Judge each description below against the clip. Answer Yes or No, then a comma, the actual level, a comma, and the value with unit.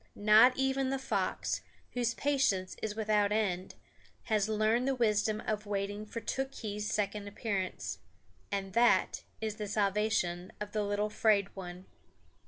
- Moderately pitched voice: No, high, 210 Hz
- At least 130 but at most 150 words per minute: Yes, average, 140 wpm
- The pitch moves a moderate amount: No, narrow, 1.7 semitones